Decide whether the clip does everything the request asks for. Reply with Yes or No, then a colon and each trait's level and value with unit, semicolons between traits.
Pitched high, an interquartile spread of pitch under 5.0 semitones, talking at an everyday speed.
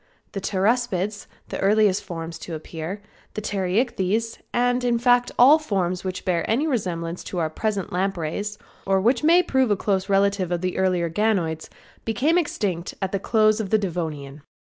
Yes: high, 195 Hz; average, 4.0 semitones; average, 160 wpm